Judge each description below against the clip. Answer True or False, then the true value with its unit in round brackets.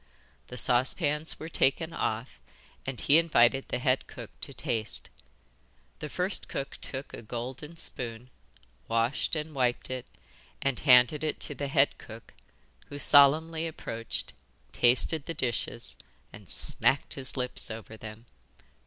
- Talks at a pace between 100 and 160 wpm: True (135 wpm)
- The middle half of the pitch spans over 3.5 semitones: True (4.1 semitones)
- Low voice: True (130 Hz)